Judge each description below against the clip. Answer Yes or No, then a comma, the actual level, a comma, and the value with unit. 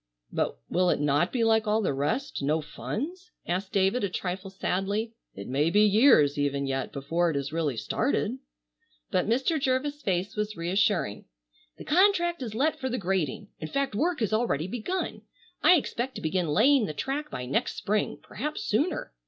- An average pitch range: No, wide, 8.2 semitones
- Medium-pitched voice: No, high, 205 Hz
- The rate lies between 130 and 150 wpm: No, average, 180 wpm